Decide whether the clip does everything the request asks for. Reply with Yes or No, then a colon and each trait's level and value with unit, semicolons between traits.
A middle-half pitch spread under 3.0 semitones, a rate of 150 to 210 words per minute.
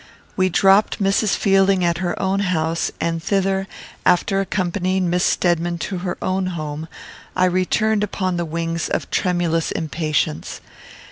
No: narrow, 2.4 semitones; average, 140 wpm